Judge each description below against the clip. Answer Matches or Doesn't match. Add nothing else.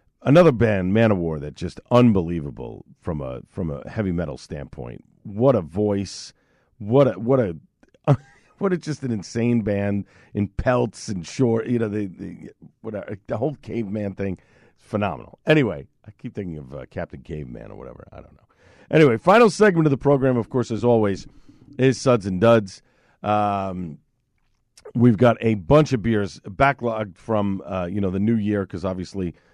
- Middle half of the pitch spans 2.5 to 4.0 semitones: Doesn't match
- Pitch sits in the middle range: Doesn't match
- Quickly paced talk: Doesn't match